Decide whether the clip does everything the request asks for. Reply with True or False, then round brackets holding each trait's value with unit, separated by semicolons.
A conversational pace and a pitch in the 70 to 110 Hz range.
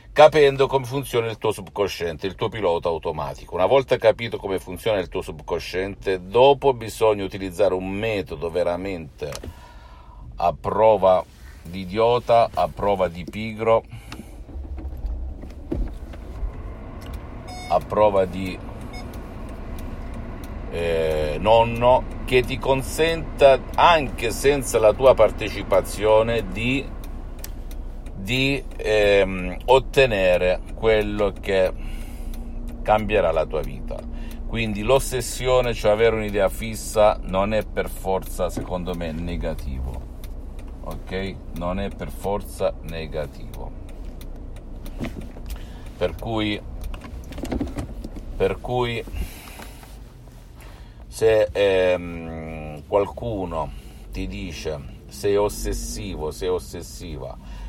False (90 wpm; 95 Hz)